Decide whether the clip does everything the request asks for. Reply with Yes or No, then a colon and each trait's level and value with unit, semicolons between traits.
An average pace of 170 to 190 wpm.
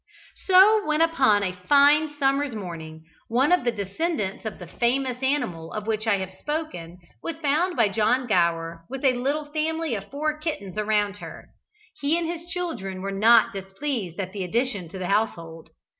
Yes: average, 175 wpm